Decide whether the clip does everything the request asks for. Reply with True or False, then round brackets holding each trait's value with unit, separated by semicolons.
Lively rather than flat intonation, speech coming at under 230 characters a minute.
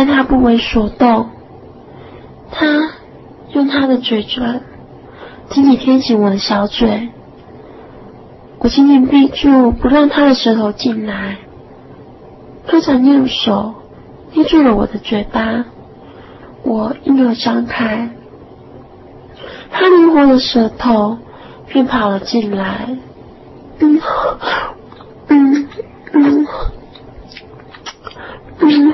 False (4.0 semitones; 135 characters per minute)